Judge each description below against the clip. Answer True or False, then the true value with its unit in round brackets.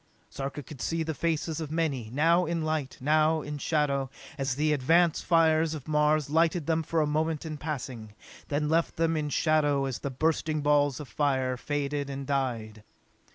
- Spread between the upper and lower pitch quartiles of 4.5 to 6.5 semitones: False (2.4 semitones)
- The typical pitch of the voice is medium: True (150 Hz)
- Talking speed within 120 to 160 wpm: False (180 wpm)